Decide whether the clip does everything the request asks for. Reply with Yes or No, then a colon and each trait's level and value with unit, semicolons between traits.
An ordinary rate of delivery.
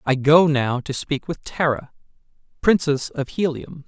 Yes: average, 155 wpm